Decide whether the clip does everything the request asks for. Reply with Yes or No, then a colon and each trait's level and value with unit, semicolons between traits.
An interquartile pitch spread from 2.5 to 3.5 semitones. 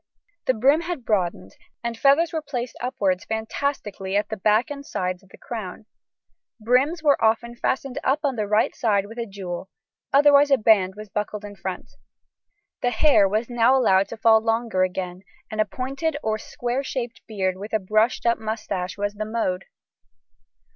No: average, 4.2 semitones